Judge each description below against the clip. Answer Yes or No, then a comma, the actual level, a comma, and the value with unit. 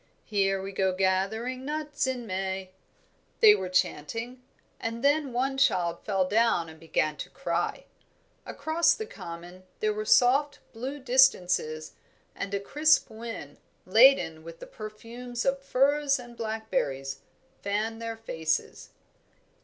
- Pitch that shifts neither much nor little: No, wide, 6.0 semitones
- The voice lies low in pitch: No, high, 225 Hz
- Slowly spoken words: Yes, slow, 130 wpm